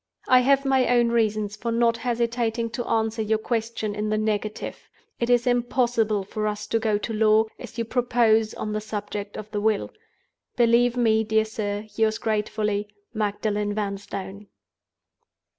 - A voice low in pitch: No, high, 220 Hz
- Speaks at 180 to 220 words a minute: No, average, 160 wpm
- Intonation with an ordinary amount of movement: No, narrow, 1.9 semitones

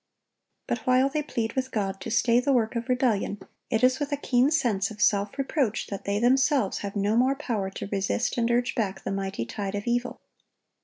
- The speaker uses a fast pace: Yes, fast, 210 wpm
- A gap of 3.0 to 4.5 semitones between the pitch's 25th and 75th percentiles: Yes, average, 4.2 semitones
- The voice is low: No, high, 235 Hz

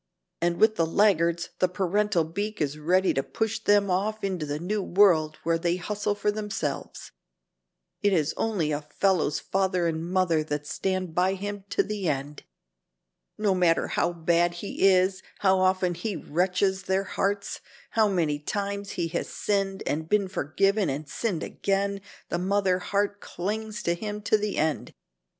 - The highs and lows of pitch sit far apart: No, average, 3.3 semitones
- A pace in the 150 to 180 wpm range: Yes, average, 165 wpm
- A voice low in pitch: No, medium, 185 Hz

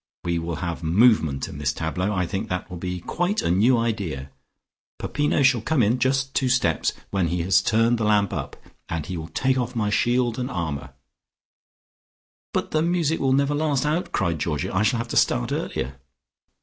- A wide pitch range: Yes, wide, 7.3 semitones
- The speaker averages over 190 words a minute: Yes, average, 200 wpm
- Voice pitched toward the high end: No, low, 105 Hz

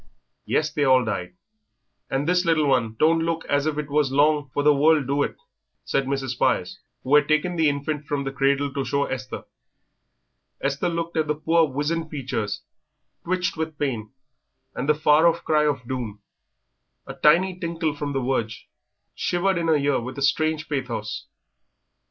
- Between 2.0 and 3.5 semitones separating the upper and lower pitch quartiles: Yes, average, 2.8 semitones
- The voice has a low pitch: No, medium, 145 Hz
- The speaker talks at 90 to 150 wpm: No, average, 175 wpm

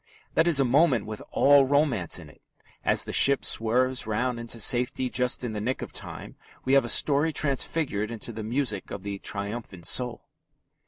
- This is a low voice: Yes, low, 125 Hz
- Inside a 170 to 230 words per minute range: Yes, average, 190 wpm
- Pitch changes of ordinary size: Yes, average, 4.1 semitones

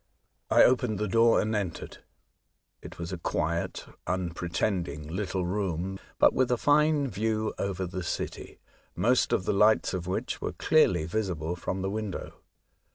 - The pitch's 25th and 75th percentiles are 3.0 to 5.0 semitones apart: Yes, average, 3.9 semitones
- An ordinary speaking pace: Yes, average, 155 wpm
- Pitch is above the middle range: No, very low, 95 Hz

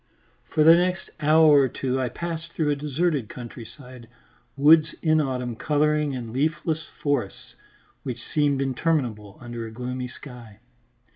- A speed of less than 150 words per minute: Yes, average, 140 wpm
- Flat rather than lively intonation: No, average, 3.9 semitones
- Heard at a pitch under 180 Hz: Yes, medium, 140 Hz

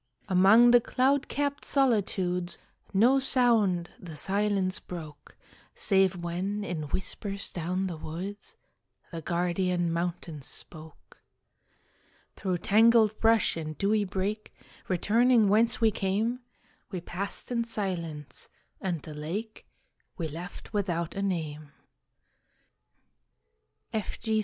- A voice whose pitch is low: No, high, 190 Hz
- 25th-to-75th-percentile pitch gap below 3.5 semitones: No, average, 4.1 semitones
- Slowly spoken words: Yes, slow, 110 wpm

